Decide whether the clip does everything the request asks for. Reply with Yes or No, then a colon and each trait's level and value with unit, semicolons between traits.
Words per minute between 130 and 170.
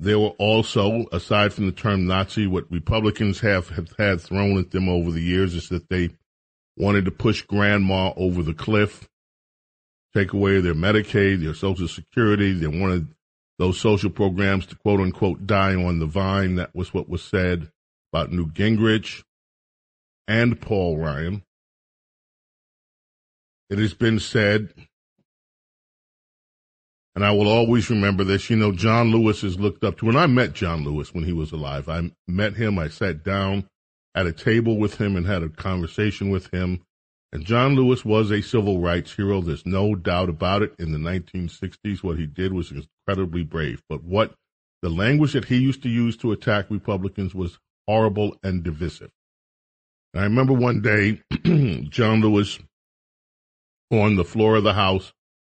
Yes: average, 165 wpm